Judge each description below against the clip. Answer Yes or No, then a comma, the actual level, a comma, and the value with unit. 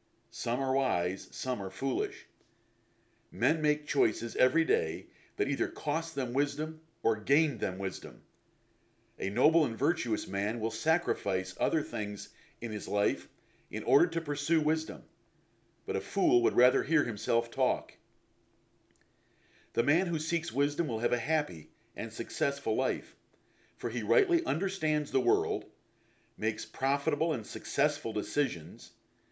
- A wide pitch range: Yes, wide, 5.7 semitones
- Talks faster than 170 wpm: No, average, 140 wpm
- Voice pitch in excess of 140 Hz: No, low, 135 Hz